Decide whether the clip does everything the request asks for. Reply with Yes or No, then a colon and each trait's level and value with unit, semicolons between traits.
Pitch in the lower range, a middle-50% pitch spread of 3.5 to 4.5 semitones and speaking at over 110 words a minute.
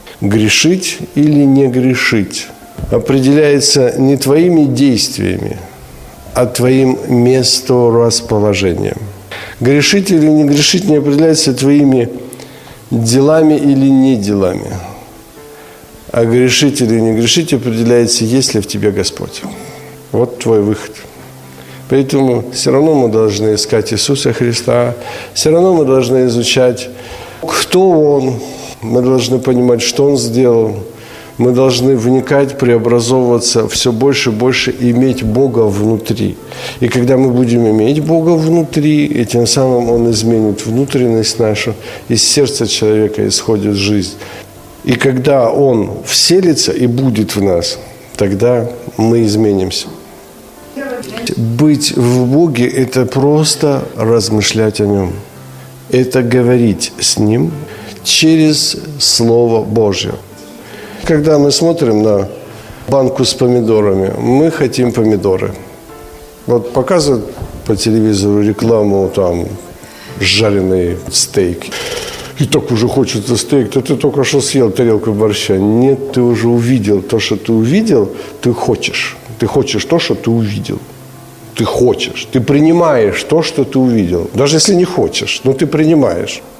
Yes: low, 120 Hz; average, 4.0 semitones; average, 120 wpm